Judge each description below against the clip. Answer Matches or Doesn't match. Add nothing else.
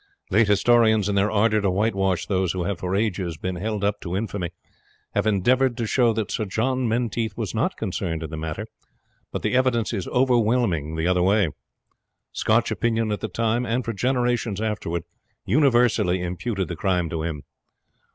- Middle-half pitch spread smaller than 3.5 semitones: Doesn't match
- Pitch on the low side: Matches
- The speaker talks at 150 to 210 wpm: Matches